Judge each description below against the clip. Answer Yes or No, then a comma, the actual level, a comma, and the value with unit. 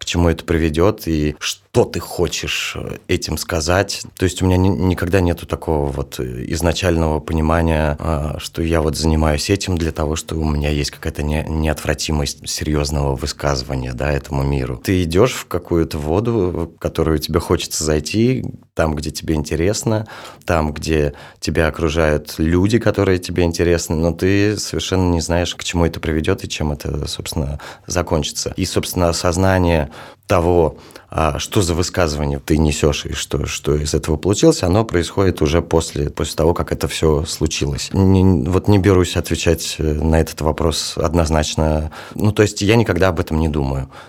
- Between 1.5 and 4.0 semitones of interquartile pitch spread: Yes, average, 2.9 semitones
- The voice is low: Yes, very low, 80 Hz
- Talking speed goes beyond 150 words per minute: Yes, fast, 160 wpm